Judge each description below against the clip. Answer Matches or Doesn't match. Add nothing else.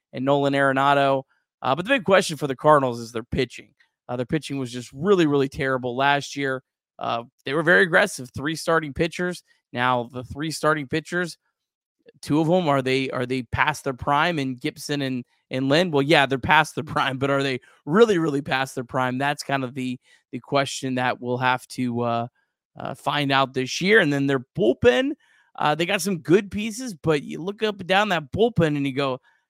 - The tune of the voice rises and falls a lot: Doesn't match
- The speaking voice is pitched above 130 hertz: Matches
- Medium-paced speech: Doesn't match